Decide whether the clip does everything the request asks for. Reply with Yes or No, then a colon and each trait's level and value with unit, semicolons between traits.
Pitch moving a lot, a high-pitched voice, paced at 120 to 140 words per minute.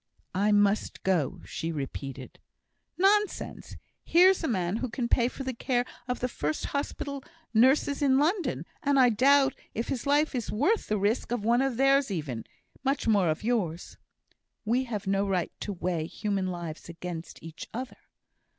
No: wide, 6.8 semitones; high, 230 Hz; average, 170 wpm